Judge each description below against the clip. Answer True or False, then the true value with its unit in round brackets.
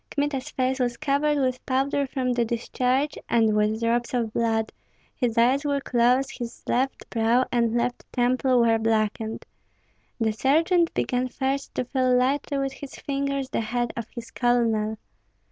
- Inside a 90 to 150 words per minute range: False (160 wpm)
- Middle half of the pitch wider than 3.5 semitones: False (2.7 semitones)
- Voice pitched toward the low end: False (250 Hz)